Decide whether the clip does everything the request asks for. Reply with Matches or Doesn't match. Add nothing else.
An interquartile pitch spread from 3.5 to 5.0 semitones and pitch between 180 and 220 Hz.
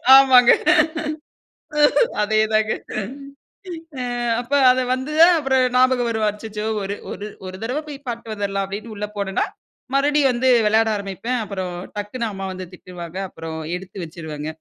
Matches